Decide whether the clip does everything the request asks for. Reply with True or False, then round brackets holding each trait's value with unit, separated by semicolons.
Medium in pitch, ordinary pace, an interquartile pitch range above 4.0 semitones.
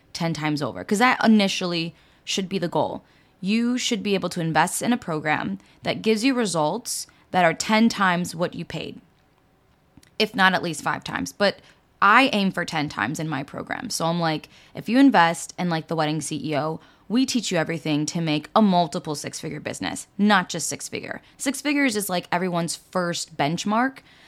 True (175 Hz; 195 wpm; 5.4 semitones)